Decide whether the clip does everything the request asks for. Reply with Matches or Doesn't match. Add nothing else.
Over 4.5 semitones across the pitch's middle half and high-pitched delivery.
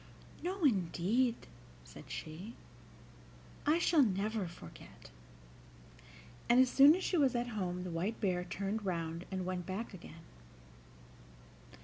Matches